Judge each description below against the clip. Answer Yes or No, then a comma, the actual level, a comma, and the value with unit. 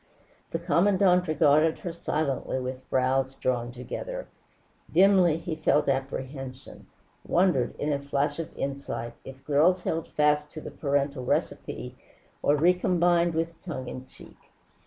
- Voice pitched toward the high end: No, medium, 150 Hz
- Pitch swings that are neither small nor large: Yes, average, 4.2 semitones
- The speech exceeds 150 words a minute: No, slow, 135 wpm